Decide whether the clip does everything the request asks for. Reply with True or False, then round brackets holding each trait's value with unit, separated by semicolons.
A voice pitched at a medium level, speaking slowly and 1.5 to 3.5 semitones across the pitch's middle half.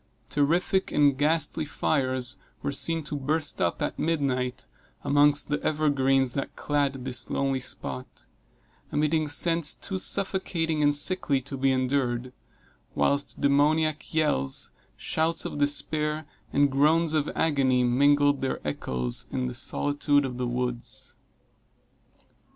True (145 Hz; 125 wpm; 2.8 semitones)